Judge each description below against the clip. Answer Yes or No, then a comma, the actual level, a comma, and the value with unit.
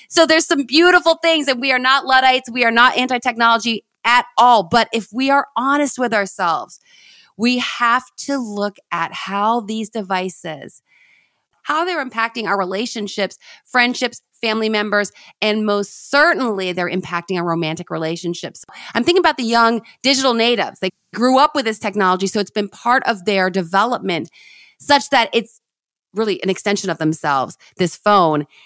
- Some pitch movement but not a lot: Yes, average, 4.6 semitones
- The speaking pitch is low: No, high, 225 Hz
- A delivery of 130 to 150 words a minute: No, average, 160 wpm